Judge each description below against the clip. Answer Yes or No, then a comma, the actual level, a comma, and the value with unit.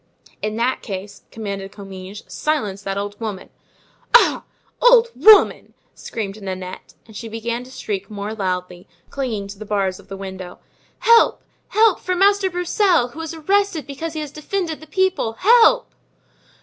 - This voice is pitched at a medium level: No, high, 230 Hz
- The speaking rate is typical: Yes, average, 155 wpm